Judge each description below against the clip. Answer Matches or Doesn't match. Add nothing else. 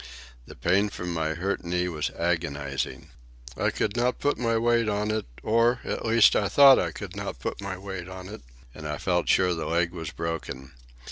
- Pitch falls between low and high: Doesn't match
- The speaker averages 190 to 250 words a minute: Matches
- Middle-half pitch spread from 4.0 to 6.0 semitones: Matches